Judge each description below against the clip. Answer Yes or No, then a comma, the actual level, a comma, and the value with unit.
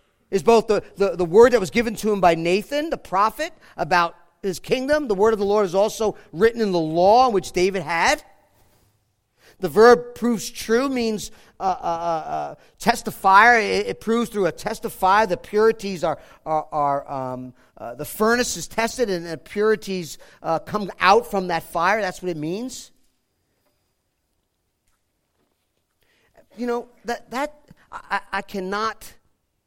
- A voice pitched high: Yes, high, 195 Hz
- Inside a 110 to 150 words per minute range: No, average, 160 wpm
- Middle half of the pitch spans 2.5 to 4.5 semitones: No, average, 5.1 semitones